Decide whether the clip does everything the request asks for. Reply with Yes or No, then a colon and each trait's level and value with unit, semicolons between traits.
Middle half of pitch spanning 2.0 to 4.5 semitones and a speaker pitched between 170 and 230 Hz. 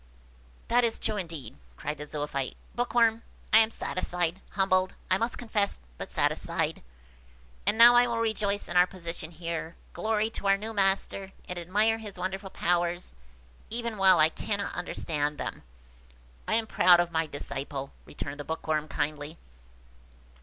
No: average, 5.2 semitones; medium, 185 Hz